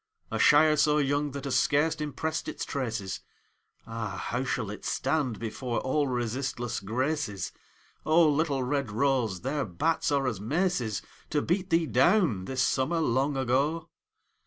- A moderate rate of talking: Yes, average, 150 wpm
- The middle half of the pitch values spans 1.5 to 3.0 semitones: No, average, 4.2 semitones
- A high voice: No, low, 135 Hz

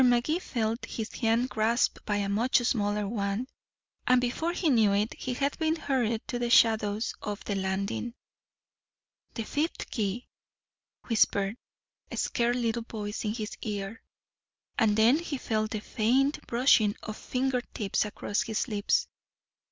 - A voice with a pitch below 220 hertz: No, high, 225 Hz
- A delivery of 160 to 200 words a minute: No, average, 150 wpm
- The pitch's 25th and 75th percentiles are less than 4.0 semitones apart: Yes, average, 3.1 semitones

